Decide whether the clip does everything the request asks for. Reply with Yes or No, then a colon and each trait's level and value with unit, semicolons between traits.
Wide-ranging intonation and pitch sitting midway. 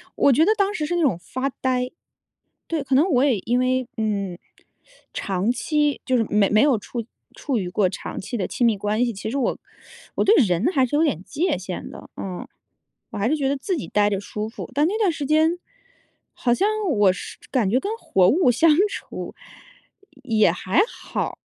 No: wide, 6.4 semitones; very high, 250 Hz